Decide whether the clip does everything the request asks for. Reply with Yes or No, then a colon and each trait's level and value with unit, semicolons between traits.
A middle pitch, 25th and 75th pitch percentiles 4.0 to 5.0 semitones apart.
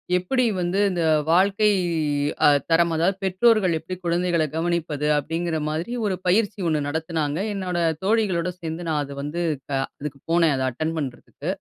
No: medium, 170 Hz; average, 2.8 semitones